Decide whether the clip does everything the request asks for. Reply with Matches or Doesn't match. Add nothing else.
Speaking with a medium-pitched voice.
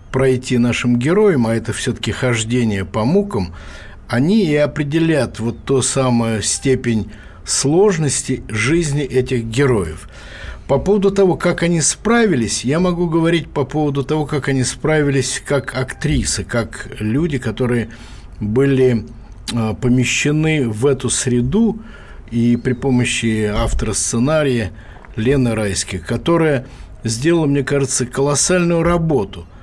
Doesn't match